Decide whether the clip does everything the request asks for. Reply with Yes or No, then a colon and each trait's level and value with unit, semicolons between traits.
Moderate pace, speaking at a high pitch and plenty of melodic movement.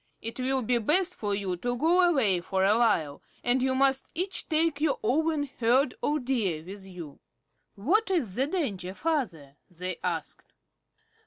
Yes: average, 165 wpm; high, 245 Hz; wide, 7.8 semitones